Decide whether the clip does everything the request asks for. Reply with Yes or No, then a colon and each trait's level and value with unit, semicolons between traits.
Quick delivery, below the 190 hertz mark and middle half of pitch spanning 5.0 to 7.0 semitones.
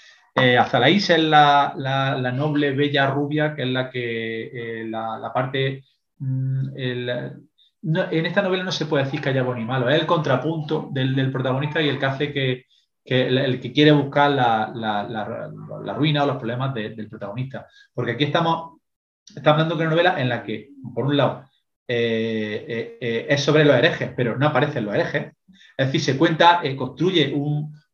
No: fast, 205 wpm; low, 135 Hz; average, 3.6 semitones